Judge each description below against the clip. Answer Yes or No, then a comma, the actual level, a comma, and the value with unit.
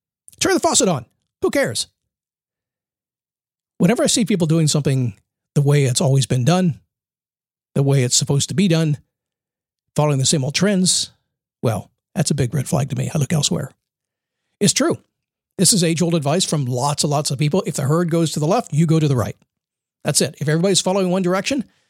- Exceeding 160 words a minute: Yes, average, 200 wpm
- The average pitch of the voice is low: No, medium, 160 Hz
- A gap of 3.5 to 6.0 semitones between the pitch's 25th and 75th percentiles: Yes, average, 4.2 semitones